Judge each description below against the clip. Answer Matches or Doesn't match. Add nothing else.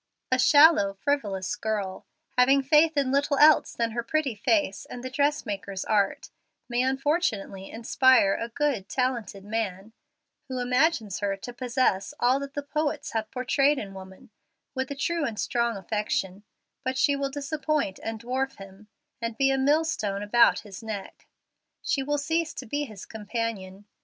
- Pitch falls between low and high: Doesn't match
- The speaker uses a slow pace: Doesn't match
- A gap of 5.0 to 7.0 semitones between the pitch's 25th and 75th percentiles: Matches